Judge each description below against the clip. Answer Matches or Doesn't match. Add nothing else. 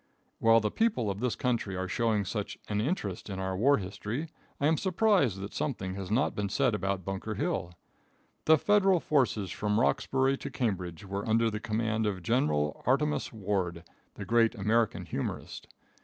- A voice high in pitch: Doesn't match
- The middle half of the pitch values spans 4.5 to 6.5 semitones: Matches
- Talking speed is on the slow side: Doesn't match